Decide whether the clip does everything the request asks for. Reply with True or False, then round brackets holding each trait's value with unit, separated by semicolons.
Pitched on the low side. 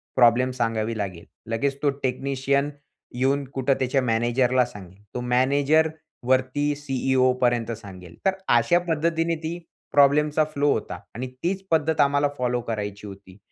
True (130 Hz)